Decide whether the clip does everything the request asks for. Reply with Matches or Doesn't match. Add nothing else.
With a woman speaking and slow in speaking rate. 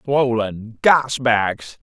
Doesn't match